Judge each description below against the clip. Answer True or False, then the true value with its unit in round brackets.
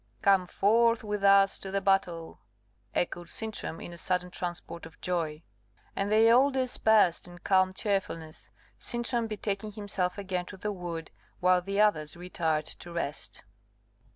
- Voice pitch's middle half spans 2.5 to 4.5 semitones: True (3.1 semitones)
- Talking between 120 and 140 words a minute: False (150 wpm)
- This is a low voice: False (190 Hz)